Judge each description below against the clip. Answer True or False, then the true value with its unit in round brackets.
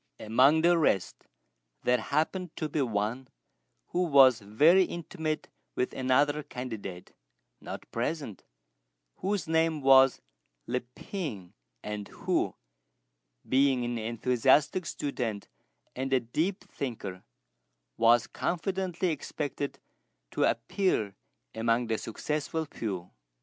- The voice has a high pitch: False (135 Hz)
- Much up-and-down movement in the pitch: True (5.7 semitones)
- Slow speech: True (105 wpm)